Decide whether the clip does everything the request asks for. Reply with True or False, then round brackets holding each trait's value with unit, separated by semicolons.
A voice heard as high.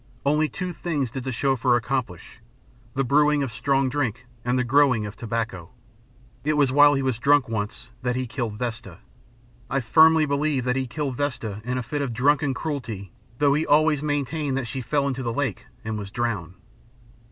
False (130 Hz)